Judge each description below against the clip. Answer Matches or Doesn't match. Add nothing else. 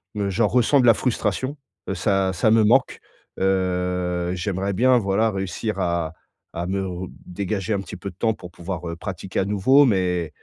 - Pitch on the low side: Matches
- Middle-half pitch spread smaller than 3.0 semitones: Doesn't match